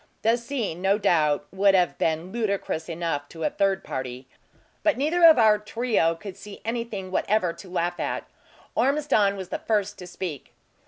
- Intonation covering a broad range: No, average, 4.8 semitones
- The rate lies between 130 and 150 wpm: No, average, 170 wpm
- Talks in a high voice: Yes, high, 195 Hz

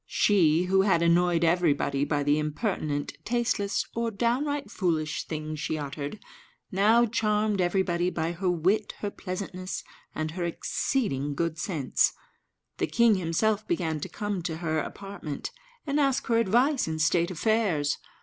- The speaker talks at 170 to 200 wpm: No, average, 145 wpm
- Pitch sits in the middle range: Yes, medium, 180 Hz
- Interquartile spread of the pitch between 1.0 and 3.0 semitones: No, average, 5.1 semitones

